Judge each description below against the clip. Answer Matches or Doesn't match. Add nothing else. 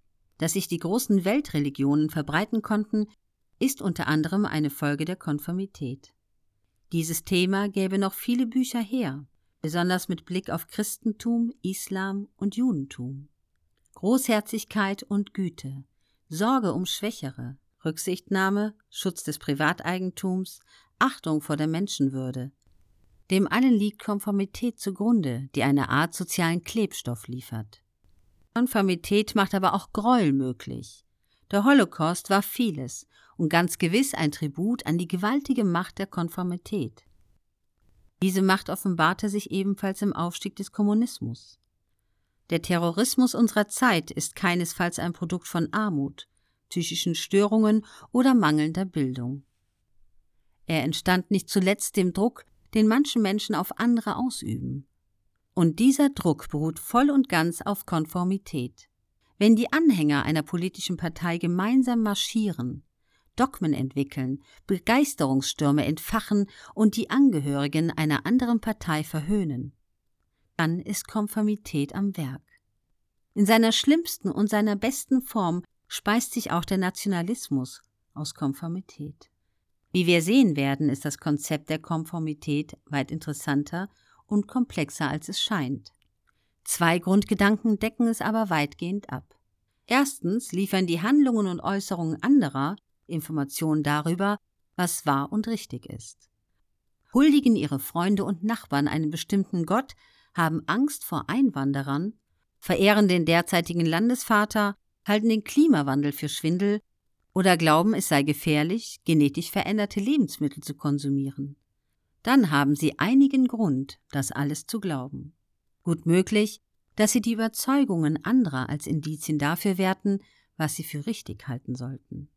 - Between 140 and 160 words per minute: Doesn't match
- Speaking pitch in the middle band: Matches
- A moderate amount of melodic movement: Doesn't match